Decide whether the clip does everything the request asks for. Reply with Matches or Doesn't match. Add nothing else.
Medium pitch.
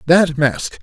Matches